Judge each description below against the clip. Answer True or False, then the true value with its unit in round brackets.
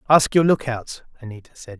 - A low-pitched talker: True (130 Hz)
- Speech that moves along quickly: False (165 wpm)